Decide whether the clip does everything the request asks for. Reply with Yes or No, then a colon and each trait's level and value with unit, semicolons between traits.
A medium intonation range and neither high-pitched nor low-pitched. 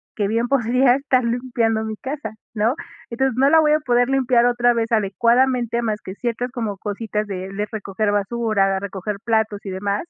No: average, 3.0 semitones; high, 230 Hz